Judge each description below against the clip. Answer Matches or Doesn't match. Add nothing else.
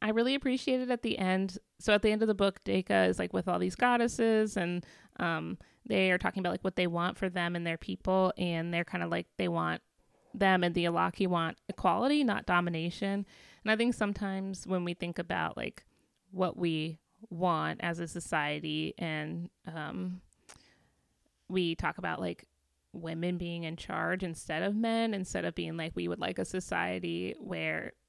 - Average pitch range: Matches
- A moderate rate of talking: Matches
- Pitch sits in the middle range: Matches